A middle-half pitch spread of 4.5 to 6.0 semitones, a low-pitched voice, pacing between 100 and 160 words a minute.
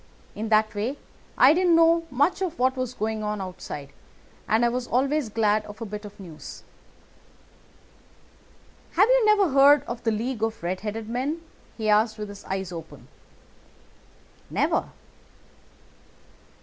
No: average, 4.9 semitones; high, 225 Hz; average, 150 wpm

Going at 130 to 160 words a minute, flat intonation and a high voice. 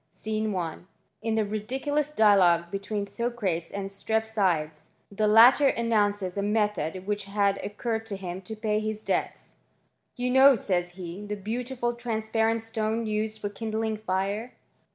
Yes: average, 155 wpm; narrow, 2.3 semitones; high, 215 Hz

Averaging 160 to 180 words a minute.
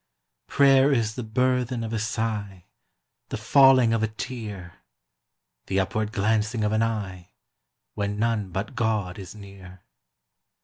No: slow, 135 wpm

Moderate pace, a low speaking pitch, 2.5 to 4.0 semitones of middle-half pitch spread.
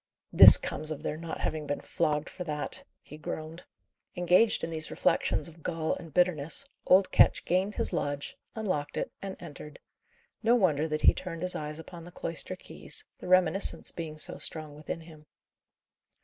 No: average, 175 wpm; medium, 160 Hz; average, 2.9 semitones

